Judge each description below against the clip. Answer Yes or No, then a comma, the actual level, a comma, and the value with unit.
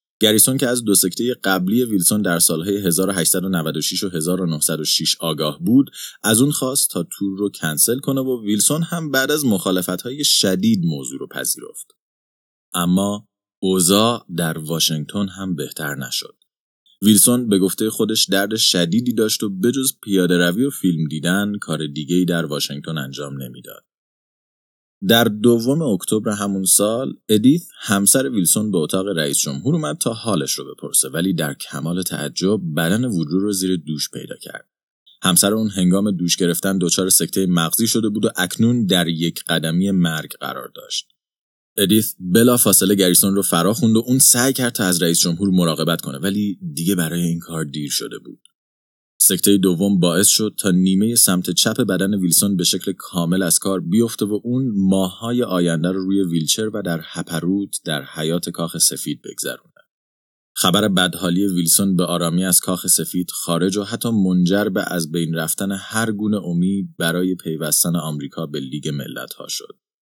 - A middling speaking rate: No, fast, 165 wpm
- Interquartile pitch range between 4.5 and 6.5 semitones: No, average, 4.1 semitones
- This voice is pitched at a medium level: No, very low, 95 Hz